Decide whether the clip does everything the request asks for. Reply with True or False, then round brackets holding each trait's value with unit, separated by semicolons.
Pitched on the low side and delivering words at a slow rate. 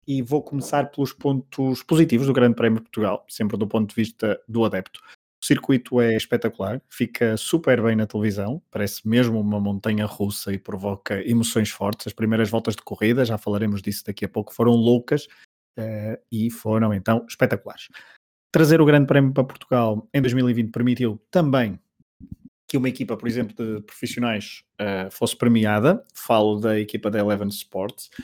False (115 Hz; 170 wpm)